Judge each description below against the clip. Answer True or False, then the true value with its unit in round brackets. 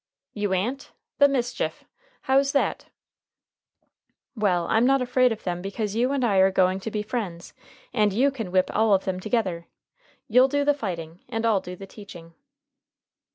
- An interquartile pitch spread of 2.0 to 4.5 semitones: False (5.1 semitones)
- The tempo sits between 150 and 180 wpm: True (170 wpm)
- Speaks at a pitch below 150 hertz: False (210 Hz)